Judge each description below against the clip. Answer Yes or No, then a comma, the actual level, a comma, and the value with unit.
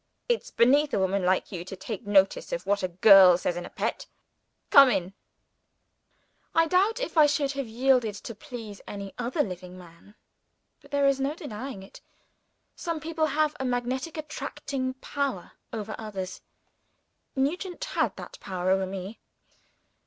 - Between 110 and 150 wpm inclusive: No, average, 160 wpm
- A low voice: No, high, 245 Hz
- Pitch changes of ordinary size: No, wide, 7.2 semitones